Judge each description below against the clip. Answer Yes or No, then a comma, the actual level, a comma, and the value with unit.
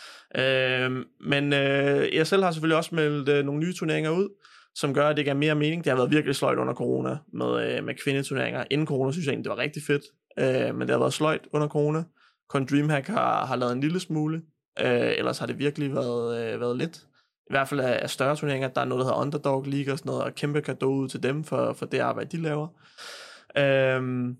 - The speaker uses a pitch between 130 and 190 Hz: Yes, medium, 140 Hz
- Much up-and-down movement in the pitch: No, narrow, 2.4 semitones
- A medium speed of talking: No, fast, 235 wpm